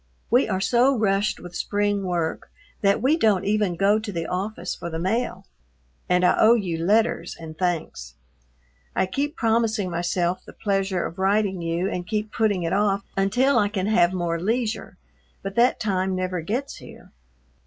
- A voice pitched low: No, high, 195 Hz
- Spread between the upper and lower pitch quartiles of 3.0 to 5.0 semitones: Yes, average, 3.3 semitones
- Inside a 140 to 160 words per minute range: No, average, 175 wpm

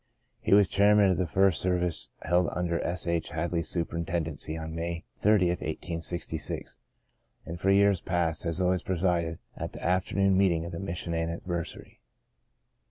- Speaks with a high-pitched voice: No, very low, 85 Hz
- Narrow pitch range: Yes, narrow, 1.9 semitones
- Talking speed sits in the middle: Yes, average, 160 wpm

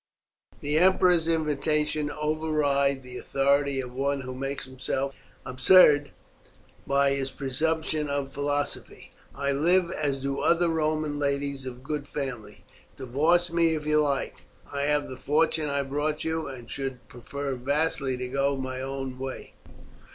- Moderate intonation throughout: No, narrow, 2.2 semitones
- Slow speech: No, average, 145 wpm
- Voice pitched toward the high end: No, medium, 140 Hz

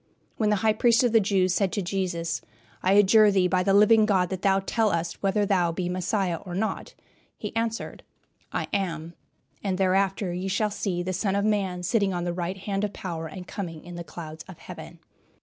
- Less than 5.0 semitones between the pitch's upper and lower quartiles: Yes, narrow, 2.6 semitones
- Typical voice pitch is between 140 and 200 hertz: Yes, high, 190 Hz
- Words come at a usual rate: No, fast, 210 wpm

